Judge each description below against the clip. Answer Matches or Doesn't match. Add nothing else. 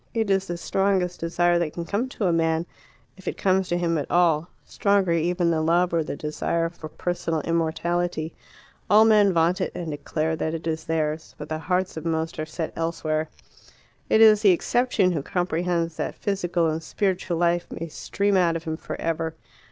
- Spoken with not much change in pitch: Matches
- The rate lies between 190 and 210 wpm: Matches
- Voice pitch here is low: Doesn't match